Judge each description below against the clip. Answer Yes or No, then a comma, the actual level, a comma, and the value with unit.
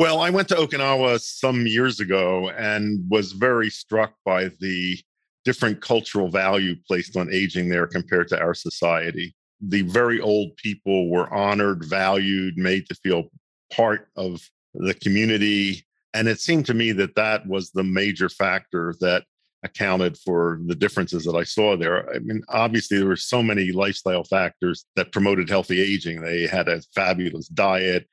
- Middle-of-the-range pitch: No, low, 100 Hz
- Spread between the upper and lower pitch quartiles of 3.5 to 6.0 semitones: No, average, 2.9 semitones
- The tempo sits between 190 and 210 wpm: No, average, 165 wpm